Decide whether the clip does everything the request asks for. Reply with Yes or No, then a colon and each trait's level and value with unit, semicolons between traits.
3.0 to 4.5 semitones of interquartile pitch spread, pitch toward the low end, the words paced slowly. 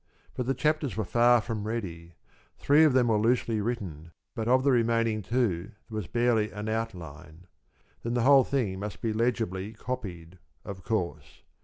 No: average, 4.2 semitones; low, 110 Hz; average, 170 wpm